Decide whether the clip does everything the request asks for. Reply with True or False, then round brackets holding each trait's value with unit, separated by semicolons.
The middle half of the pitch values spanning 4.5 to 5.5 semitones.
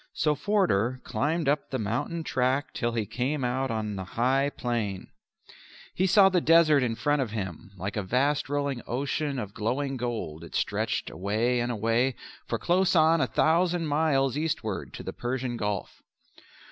True (4.8 semitones)